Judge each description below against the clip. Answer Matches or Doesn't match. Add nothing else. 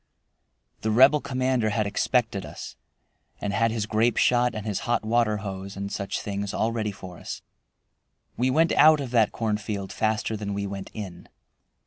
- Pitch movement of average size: Matches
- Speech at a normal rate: Matches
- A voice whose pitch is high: Doesn't match